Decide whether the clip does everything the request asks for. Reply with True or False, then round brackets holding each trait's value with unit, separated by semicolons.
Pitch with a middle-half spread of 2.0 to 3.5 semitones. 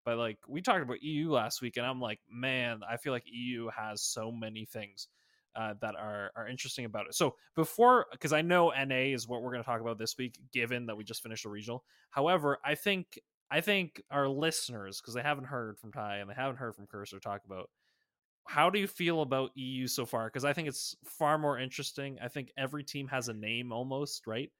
False (4.1 semitones)